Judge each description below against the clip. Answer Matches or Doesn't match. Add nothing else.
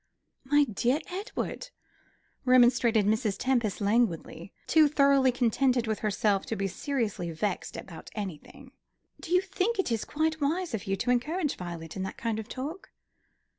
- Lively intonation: Matches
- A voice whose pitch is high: Matches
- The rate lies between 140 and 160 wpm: Matches